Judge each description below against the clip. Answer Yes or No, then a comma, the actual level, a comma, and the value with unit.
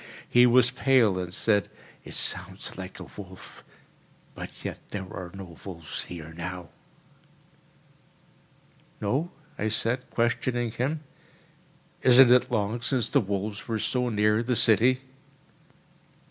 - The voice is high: No, low, 110 Hz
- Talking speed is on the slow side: Yes, slow, 120 wpm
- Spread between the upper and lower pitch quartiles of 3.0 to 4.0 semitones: No, average, 4.6 semitones